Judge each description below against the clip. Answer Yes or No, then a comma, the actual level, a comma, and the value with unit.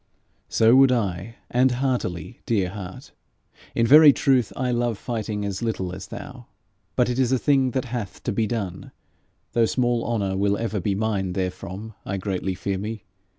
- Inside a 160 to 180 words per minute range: Yes, average, 175 wpm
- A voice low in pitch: Yes, low, 110 Hz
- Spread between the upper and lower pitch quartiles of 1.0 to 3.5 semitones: No, average, 4.1 semitones